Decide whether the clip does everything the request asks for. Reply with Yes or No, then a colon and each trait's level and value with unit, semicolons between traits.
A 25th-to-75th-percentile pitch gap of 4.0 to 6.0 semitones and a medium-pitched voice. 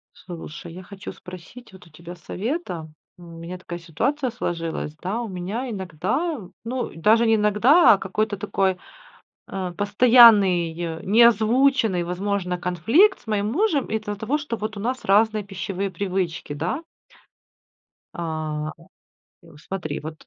No: average, 4.7 semitones; high, 195 Hz